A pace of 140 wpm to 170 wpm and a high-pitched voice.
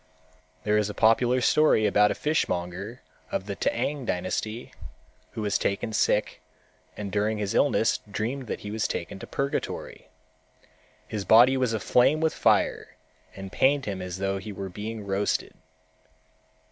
No: average, 150 wpm; low, 105 Hz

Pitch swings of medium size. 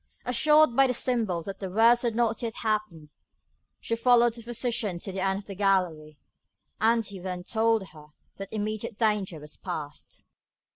Yes: average, 3.9 semitones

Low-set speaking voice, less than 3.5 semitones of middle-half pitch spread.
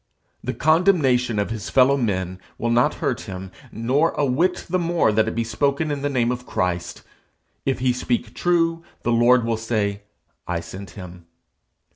No: low, 120 Hz; average, 5.2 semitones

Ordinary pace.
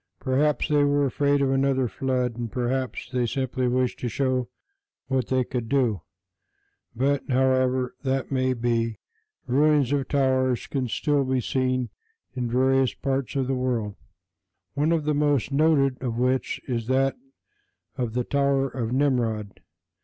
Yes: average, 150 wpm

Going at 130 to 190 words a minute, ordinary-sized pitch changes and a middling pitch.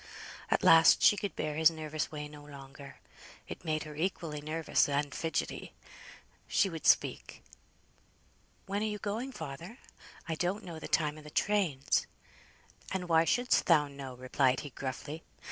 Yes: average, 160 wpm; average, 3.3 semitones; medium, 155 Hz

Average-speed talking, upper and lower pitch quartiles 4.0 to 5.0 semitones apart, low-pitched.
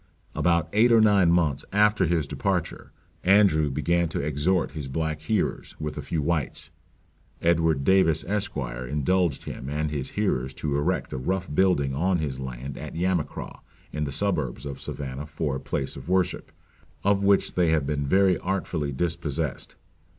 Yes: average, 165 wpm; average, 4.6 semitones; very low, 80 Hz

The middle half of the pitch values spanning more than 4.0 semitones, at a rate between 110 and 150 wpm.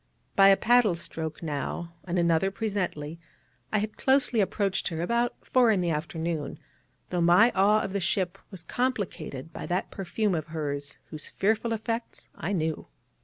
No: average, 4.7 semitones; average, 165 wpm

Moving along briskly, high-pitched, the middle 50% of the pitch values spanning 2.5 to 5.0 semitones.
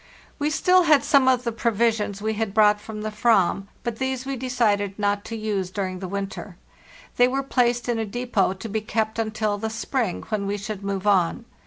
Yes: fast, 215 wpm; high, 220 Hz; average, 3.1 semitones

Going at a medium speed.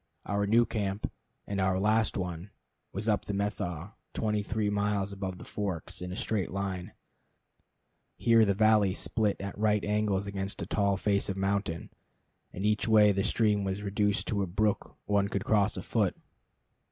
Yes: average, 170 wpm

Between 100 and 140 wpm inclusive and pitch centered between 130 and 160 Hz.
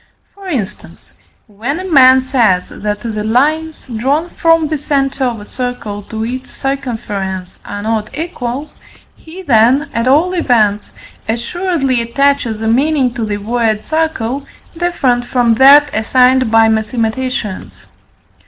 No: slow, 135 wpm; very high, 250 Hz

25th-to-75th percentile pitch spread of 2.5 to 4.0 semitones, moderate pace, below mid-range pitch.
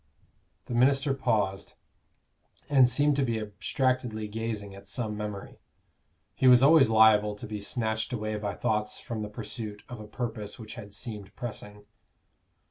Yes: average, 2.9 semitones; average, 150 wpm; low, 110 Hz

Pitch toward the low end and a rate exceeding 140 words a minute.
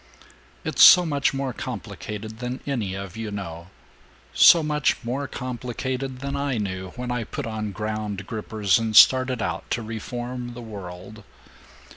Yes: low, 115 Hz; average, 150 wpm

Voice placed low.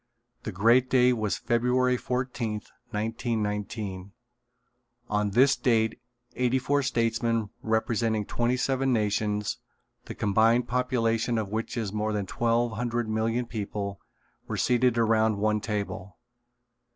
Yes: low, 115 Hz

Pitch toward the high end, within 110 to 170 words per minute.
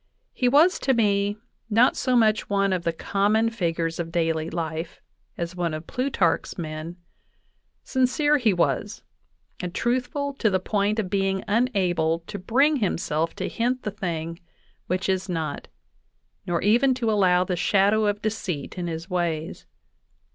Yes: high, 195 Hz; average, 155 wpm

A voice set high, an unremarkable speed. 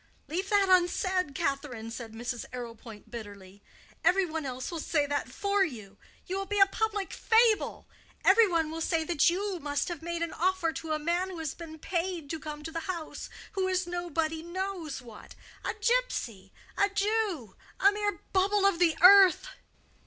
Yes: very high, 340 Hz; average, 175 wpm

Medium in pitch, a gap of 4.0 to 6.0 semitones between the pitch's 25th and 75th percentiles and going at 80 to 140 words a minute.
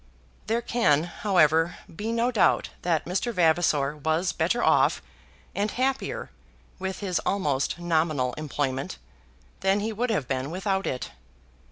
Yes: medium, 175 Hz; average, 5.3 semitones; slow, 135 wpm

